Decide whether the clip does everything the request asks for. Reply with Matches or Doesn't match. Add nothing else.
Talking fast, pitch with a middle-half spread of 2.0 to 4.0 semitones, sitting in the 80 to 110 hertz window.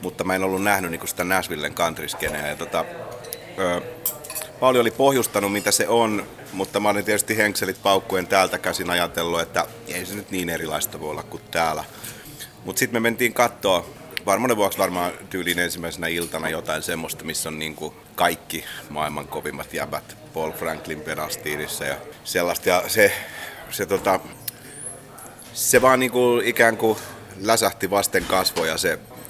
Doesn't match